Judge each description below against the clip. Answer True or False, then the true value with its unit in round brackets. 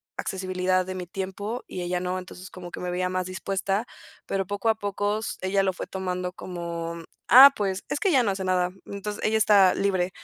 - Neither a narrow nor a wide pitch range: False (1.8 semitones)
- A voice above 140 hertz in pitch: True (190 Hz)